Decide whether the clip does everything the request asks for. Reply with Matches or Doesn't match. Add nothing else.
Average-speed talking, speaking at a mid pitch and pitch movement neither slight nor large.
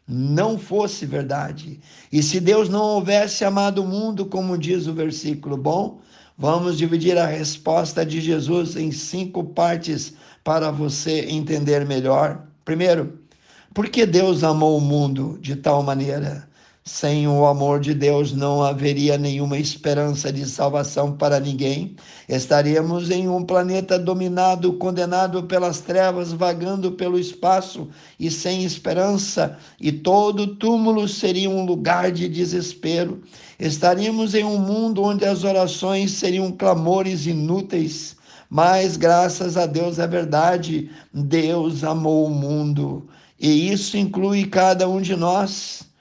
Matches